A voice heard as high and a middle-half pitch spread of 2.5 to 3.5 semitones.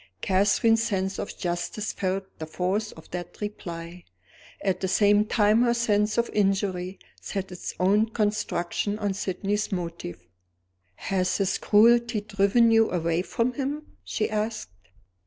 Yes: high, 200 Hz; average, 2.9 semitones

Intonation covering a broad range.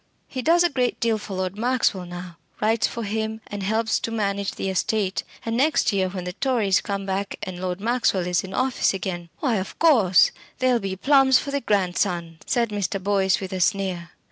No: average, 3.7 semitones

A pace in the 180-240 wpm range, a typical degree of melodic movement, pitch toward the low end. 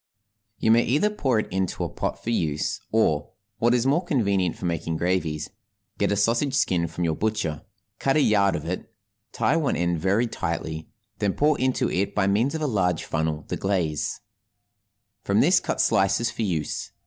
No: average, 185 wpm; wide, 5.9 semitones; low, 100 Hz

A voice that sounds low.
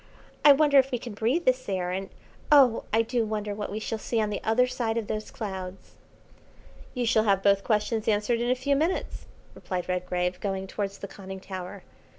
No: high, 215 Hz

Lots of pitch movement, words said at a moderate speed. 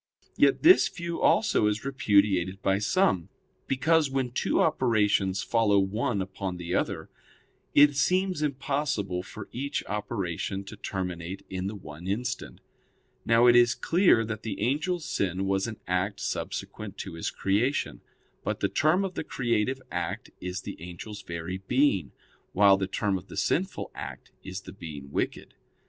Yes: wide, 5.9 semitones; average, 155 wpm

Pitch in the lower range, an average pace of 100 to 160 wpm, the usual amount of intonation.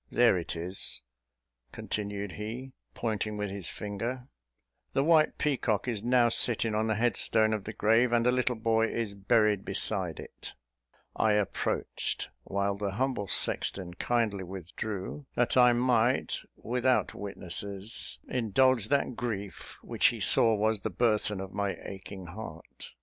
Yes: low, 110 Hz; average, 145 wpm; average, 3.3 semitones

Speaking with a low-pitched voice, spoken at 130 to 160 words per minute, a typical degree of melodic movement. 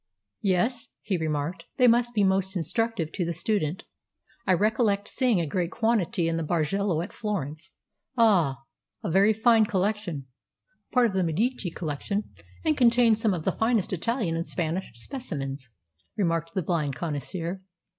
No: high, 190 Hz; average, 155 wpm; average, 5.0 semitones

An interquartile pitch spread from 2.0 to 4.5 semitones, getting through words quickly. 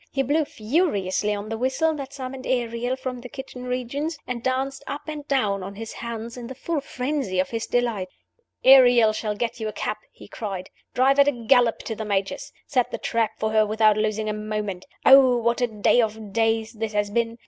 Yes: average, 3.4 semitones; fast, 210 wpm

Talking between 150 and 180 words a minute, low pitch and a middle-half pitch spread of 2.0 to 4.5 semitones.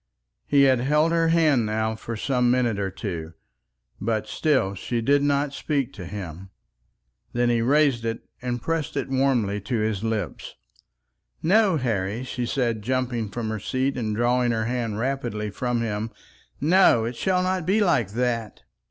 Yes: average, 165 wpm; low, 120 Hz; average, 4.1 semitones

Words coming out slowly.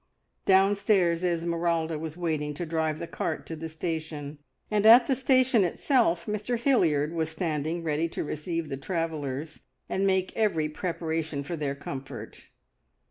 No: average, 145 wpm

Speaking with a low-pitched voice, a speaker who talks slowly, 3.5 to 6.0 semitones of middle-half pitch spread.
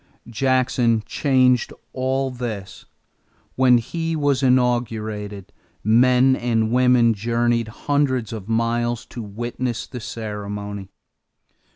No: low, 120 Hz; slow, 95 wpm; narrow, 2.6 semitones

